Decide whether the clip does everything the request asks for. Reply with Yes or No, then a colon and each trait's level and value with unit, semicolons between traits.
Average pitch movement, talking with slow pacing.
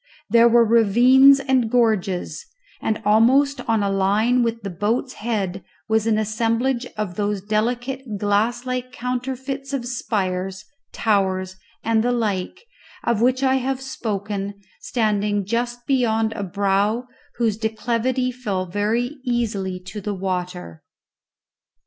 Yes: average, 3.3 semitones; slow, 130 wpm